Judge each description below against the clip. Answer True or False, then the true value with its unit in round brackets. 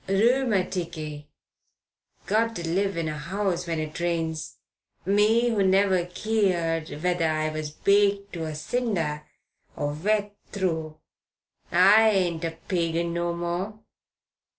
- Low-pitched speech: False (175 Hz)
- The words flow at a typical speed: False (125 wpm)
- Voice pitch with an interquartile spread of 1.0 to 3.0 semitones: False (3.7 semitones)